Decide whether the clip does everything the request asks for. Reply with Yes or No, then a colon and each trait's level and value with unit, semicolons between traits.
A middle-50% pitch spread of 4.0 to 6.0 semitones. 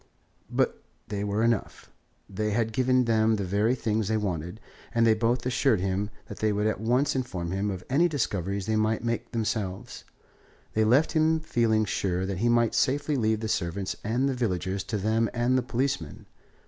No: average, 3.3 semitones